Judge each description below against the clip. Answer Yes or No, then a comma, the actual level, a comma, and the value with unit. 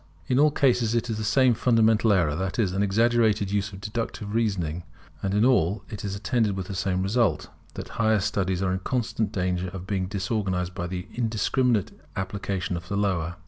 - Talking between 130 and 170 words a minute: No, average, 200 wpm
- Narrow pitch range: No, average, 3.3 semitones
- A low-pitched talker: Yes, low, 100 Hz